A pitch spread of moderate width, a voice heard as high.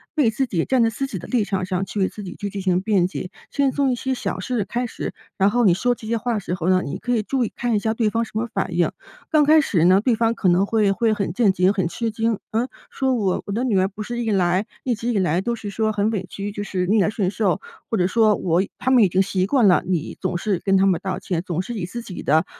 Yes: average, 3.8 semitones; high, 205 Hz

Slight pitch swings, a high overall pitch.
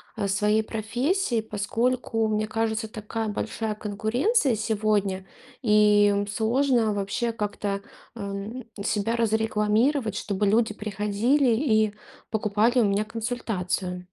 Yes: narrow, 1.9 semitones; high, 215 Hz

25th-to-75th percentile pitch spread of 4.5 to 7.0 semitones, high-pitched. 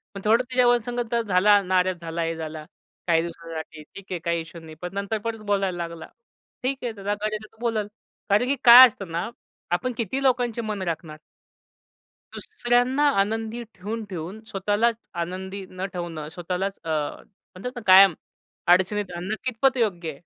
Yes: average, 4.8 semitones; high, 195 Hz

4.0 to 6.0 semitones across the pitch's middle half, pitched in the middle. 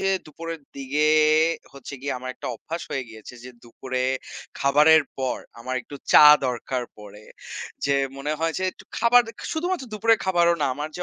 Yes: average, 4.9 semitones; medium, 145 Hz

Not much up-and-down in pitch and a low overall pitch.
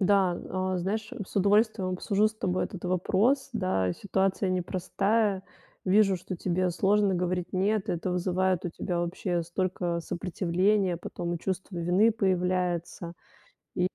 No: narrow, 2.0 semitones; medium, 185 Hz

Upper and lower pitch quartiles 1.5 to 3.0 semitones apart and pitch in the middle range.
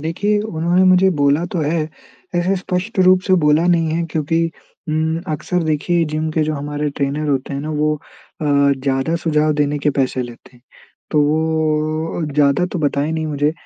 Yes: narrow, 2.4 semitones; medium, 155 Hz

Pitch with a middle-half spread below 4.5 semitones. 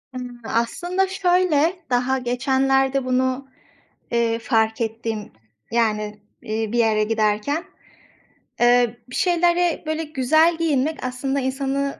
No: average, 4.9 semitones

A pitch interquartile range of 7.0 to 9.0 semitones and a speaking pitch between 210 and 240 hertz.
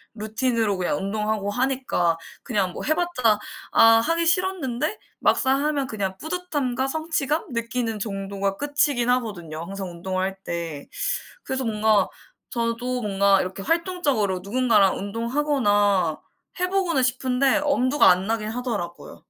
No: wide, 5.5 semitones; high, 230 Hz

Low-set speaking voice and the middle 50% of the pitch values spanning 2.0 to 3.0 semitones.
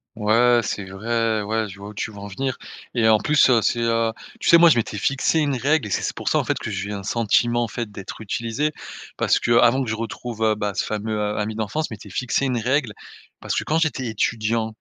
Yes: low, 115 Hz; narrow, 2.6 semitones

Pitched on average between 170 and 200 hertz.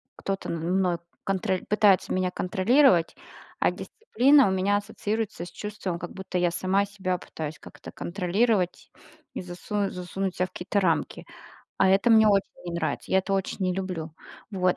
Yes: high, 190 Hz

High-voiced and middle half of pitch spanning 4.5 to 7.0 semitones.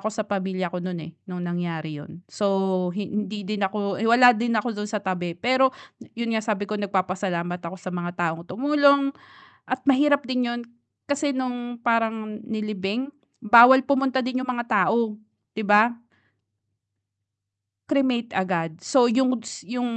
Yes: high, 215 Hz; average, 4.9 semitones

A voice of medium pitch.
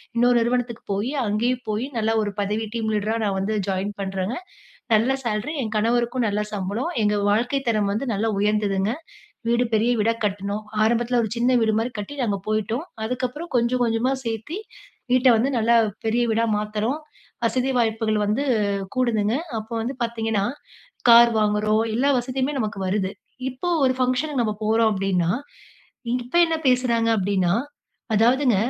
No: high, 225 Hz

